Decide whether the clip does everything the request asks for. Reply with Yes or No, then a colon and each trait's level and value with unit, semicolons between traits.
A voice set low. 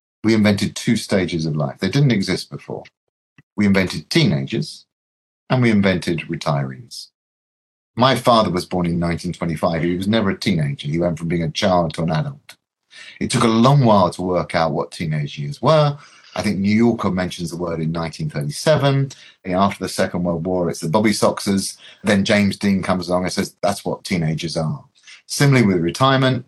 Yes: low, 100 Hz